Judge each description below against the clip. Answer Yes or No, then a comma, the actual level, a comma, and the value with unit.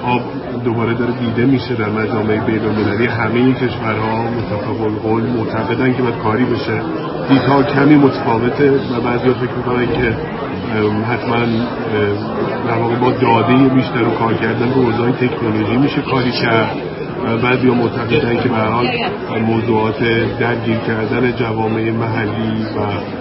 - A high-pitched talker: No, low, 115 Hz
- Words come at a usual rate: Yes, average, 145 wpm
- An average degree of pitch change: No, narrow, 1.9 semitones